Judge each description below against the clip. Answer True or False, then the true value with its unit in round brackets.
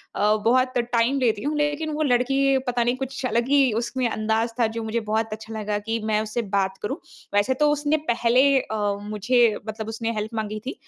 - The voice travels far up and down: False (3.3 semitones)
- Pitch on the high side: True (235 Hz)